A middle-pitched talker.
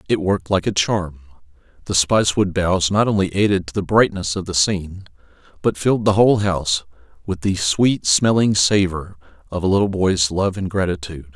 No: very low, 90 Hz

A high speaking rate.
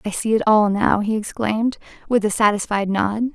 No: average, 195 wpm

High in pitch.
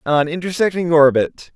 No: medium, 160 Hz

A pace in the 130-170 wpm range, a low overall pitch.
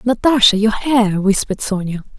No: average, 140 wpm; high, 215 Hz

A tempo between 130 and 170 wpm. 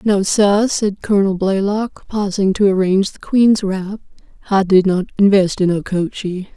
Yes: average, 155 wpm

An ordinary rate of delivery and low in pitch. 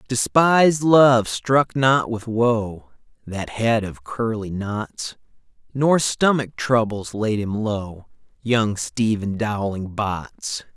No: slow, 115 wpm; low, 115 Hz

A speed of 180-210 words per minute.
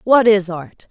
Yes: average, 200 wpm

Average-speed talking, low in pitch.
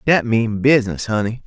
Yes: average, 165 wpm; low, 115 Hz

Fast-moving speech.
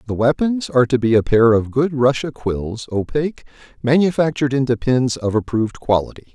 No: average, 170 wpm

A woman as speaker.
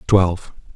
No: male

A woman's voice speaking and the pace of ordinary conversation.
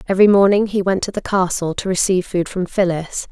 No: female; fast, 215 wpm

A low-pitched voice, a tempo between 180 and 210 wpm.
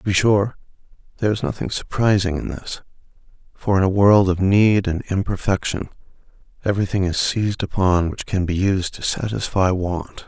No: very low, 95 Hz; average, 165 wpm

